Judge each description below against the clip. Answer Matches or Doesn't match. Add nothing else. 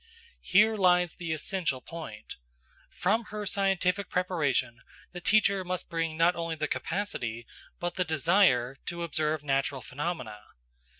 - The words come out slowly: Matches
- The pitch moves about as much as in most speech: Matches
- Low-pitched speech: Doesn't match